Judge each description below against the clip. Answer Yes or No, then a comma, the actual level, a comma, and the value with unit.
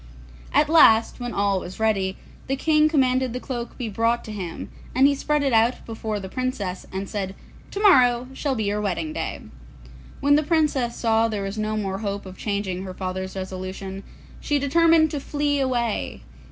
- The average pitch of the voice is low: No, high, 230 Hz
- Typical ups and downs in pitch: No, wide, 5.8 semitones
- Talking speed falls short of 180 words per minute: No, average, 190 wpm